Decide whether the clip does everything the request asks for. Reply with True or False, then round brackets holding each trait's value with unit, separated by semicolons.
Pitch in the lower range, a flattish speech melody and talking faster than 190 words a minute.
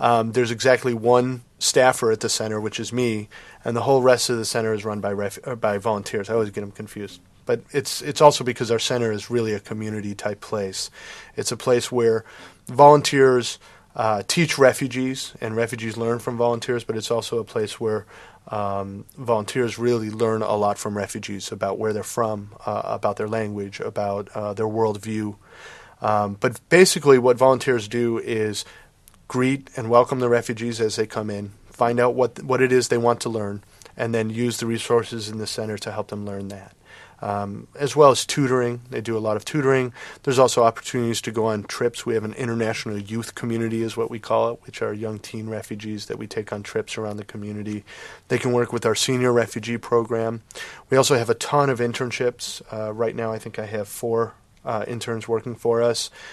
True (115 Hz; 2.3 semitones; 205 wpm)